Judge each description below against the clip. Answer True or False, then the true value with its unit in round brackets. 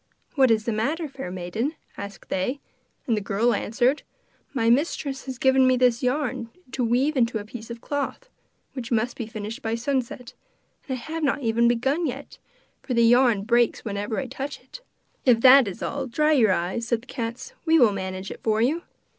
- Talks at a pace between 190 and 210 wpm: True (195 wpm)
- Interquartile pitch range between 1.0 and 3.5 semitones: True (3.2 semitones)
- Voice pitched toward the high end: True (240 Hz)